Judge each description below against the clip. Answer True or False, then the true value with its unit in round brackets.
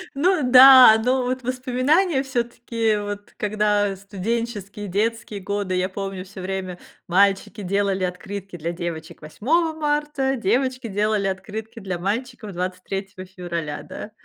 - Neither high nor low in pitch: False (205 Hz)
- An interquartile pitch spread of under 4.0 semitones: False (4.7 semitones)